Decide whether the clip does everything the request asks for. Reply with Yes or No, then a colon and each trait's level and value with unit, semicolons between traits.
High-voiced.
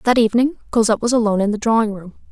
Yes: high, 220 Hz